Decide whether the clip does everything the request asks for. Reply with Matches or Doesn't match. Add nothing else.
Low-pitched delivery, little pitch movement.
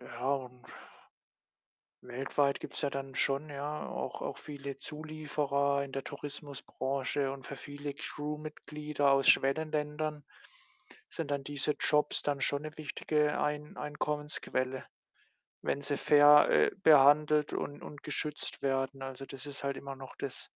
Doesn't match